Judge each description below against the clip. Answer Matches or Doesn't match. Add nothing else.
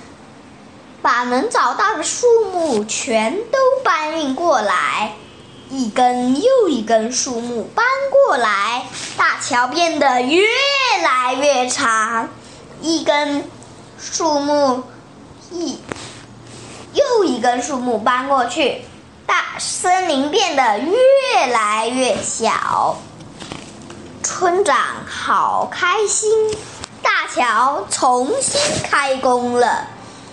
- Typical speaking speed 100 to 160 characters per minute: Matches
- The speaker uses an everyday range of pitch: Doesn't match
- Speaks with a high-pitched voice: Matches